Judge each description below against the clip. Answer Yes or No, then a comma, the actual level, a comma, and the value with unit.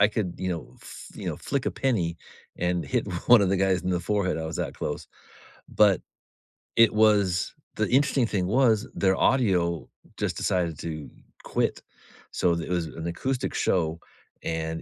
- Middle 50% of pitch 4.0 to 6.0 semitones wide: Yes, average, 4.3 semitones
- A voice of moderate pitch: No, very low, 95 Hz